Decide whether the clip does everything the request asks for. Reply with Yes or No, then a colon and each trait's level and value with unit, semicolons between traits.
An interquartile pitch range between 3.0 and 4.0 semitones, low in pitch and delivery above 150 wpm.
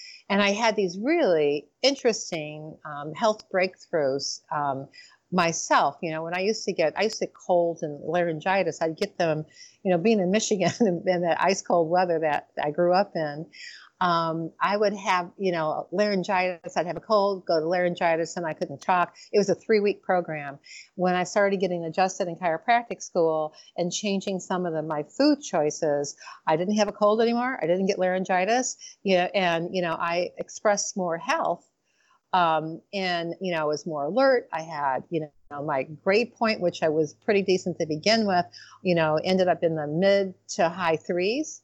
No: average, 3.6 semitones; medium, 180 Hz; average, 195 wpm